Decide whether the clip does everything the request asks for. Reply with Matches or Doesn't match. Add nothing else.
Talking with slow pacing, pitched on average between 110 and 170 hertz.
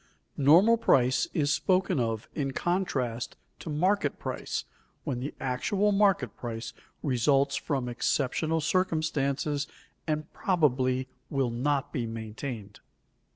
Matches